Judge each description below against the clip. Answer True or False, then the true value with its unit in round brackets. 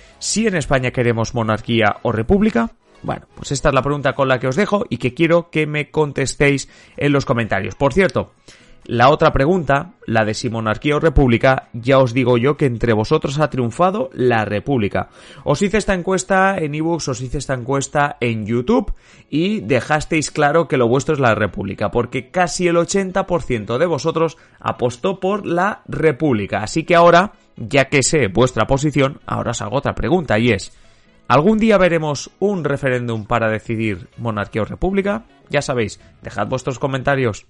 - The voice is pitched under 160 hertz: True (140 Hz)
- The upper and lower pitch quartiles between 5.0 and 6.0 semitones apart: True (5.6 semitones)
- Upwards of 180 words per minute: False (175 wpm)